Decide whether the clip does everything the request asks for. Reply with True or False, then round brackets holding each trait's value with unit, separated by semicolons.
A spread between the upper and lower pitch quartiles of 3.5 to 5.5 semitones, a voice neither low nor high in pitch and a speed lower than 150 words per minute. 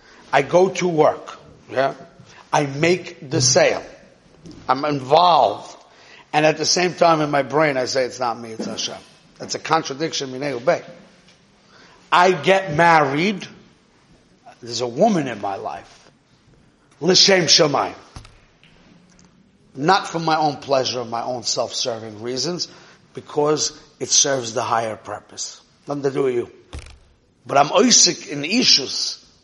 True (4.4 semitones; 155 Hz; 140 wpm)